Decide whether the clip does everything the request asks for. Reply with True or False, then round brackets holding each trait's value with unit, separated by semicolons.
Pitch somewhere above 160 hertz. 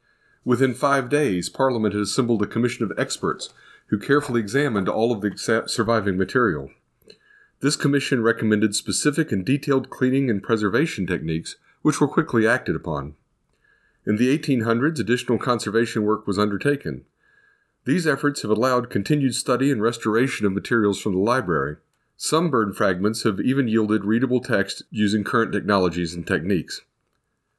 False (115 Hz)